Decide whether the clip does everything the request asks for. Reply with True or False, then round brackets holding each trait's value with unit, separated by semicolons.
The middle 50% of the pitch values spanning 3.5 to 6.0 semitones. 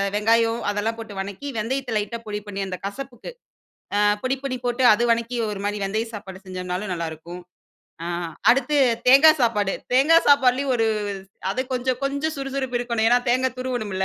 True (4.0 semitones)